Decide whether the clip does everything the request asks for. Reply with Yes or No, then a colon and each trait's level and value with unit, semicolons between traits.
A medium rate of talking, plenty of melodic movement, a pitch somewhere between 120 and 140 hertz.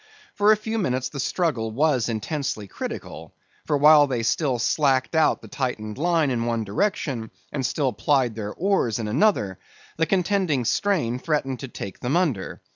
Yes: average, 170 wpm; wide, 5.7 semitones; low, 135 Hz